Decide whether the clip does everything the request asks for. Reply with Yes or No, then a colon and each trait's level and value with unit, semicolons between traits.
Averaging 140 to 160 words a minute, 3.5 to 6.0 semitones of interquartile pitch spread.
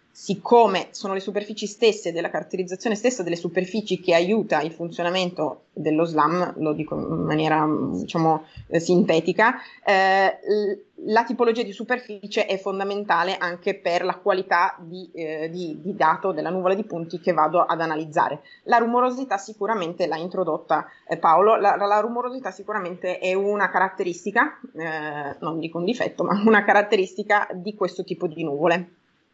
Yes: average, 150 wpm; average, 3.8 semitones